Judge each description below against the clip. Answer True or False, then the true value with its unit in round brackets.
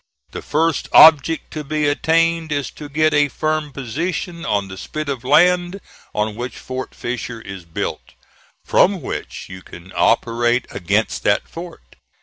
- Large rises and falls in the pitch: True (5.7 semitones)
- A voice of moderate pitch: True (145 Hz)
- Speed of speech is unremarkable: True (150 wpm)